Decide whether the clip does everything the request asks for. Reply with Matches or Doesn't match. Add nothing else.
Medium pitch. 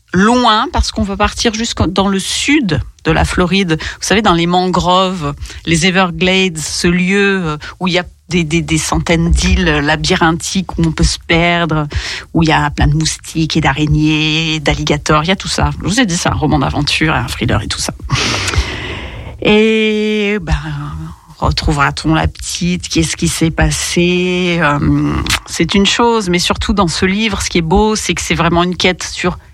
Matches